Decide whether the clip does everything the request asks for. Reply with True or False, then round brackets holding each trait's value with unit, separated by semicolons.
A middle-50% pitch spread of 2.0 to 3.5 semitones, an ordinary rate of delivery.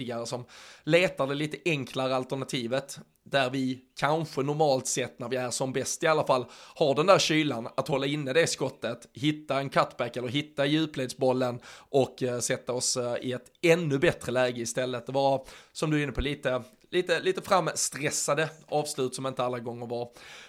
True (3.0 semitones; 175 wpm)